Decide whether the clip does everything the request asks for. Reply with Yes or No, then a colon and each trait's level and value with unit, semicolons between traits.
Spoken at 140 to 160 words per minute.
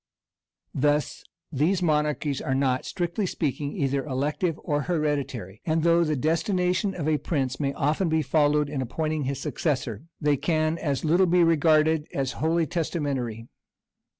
Yes: average, 150 wpm